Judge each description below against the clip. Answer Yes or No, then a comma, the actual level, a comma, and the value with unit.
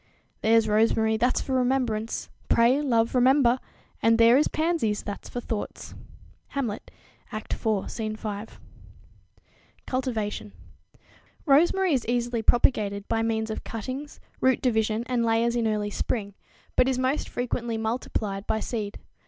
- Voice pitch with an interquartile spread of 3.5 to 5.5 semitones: No, average, 2.7 semitones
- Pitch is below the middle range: No, high, 230 Hz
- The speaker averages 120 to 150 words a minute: Yes, slow, 135 wpm